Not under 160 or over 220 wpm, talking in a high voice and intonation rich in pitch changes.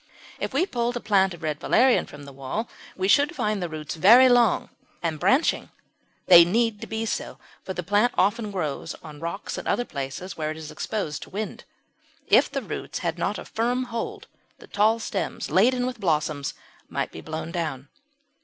Yes: average, 190 wpm; high, 195 Hz; wide, 6.6 semitones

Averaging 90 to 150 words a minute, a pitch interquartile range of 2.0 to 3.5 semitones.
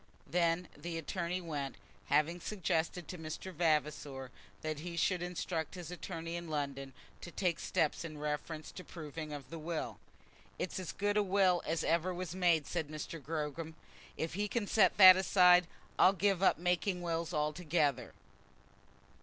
No: average, 160 wpm; average, 2.7 semitones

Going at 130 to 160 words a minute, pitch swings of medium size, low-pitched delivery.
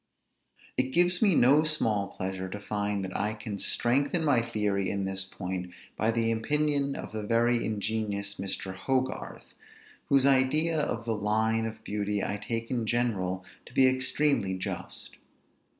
Yes: average, 155 wpm; average, 4.4 semitones; low, 110 Hz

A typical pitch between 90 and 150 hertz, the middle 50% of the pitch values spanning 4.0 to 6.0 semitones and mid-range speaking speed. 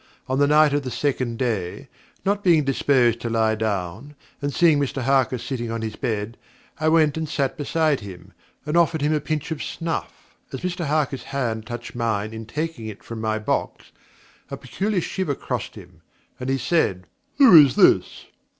Yes: low, 135 Hz; wide, 5.4 semitones; average, 185 wpm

